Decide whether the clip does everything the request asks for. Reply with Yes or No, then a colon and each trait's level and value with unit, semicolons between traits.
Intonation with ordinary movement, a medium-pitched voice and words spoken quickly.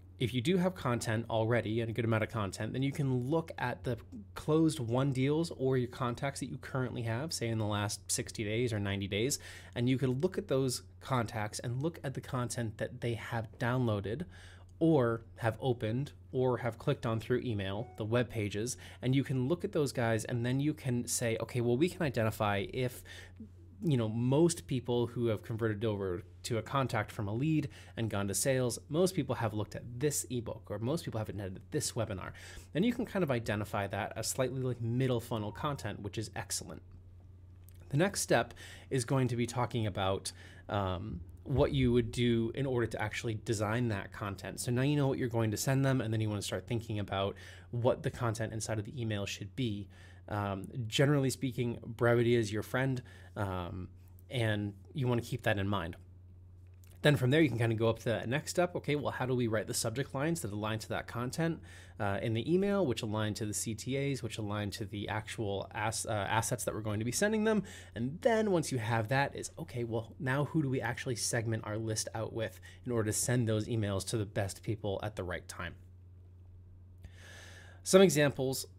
No: average, 4.2 semitones; low, 115 Hz; fast, 215 wpm